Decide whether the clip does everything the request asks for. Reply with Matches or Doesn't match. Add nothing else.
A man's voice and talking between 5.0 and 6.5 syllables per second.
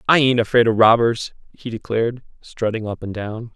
Matches